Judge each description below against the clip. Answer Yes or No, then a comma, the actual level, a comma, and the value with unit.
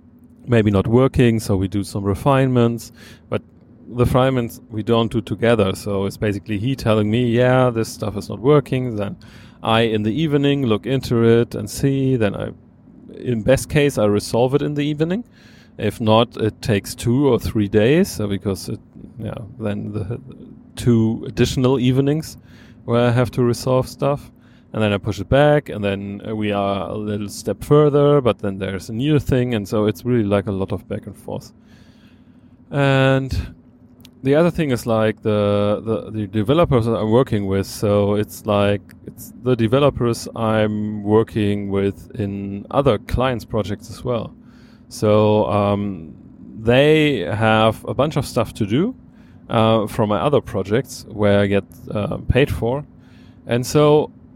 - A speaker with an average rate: Yes, average, 170 wpm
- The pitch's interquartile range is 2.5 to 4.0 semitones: Yes, average, 3.4 semitones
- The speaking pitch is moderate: No, low, 115 Hz